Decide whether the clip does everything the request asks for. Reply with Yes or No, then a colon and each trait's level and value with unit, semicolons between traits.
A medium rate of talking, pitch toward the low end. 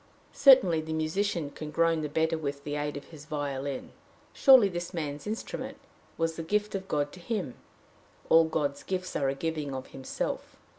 No: average, 180 wpm; medium, 160 Hz